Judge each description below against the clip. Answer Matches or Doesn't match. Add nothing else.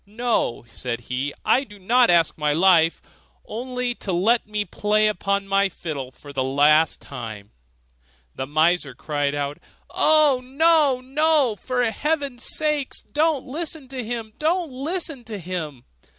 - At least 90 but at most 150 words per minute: Matches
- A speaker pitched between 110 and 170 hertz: Doesn't match